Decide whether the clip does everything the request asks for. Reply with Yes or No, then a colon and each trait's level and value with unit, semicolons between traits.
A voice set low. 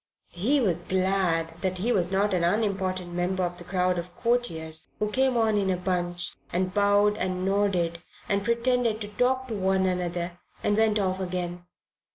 No: high, 190 Hz